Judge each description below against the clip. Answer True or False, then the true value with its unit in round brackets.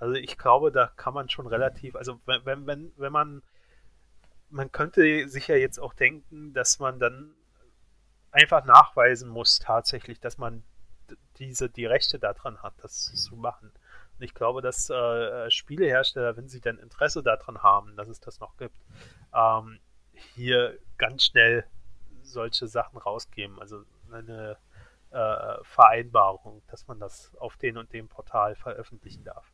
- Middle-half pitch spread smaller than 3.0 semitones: False (3.7 semitones)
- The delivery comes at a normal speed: True (150 wpm)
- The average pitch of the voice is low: True (115 Hz)